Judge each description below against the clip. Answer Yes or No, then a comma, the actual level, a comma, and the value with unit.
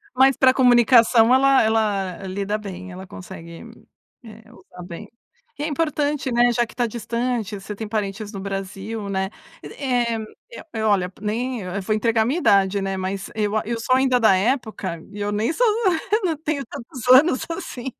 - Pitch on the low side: No, high, 220 Hz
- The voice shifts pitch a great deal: No, average, 4.3 semitones